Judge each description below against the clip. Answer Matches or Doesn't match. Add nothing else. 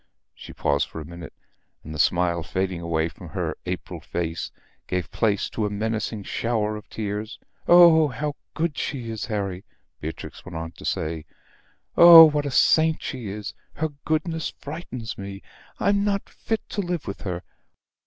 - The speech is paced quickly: Doesn't match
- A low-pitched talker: Matches